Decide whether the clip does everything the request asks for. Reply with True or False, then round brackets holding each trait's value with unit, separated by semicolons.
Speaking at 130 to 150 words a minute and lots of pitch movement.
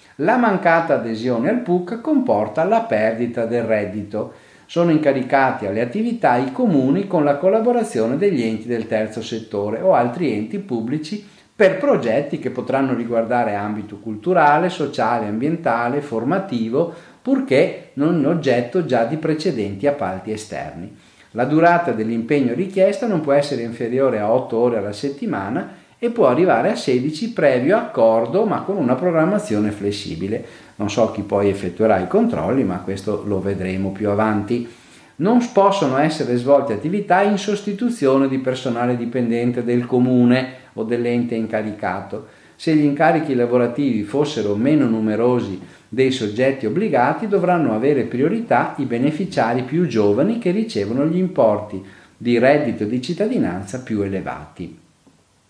True (135 wpm; 7.2 semitones)